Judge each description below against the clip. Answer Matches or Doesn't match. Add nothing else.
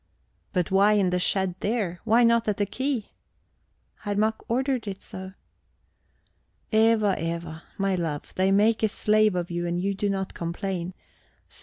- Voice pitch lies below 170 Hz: Doesn't match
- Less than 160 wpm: Doesn't match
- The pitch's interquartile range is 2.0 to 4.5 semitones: Matches